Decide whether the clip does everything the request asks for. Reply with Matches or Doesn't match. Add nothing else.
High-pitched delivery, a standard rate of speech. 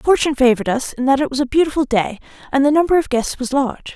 Doesn't match